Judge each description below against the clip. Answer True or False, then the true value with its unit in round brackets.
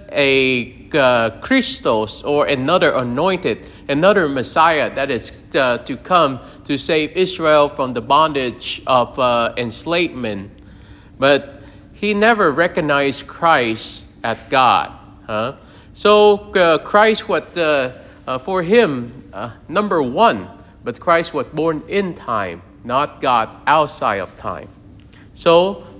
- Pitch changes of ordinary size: False (7.4 semitones)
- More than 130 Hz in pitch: True (140 Hz)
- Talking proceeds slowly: True (120 wpm)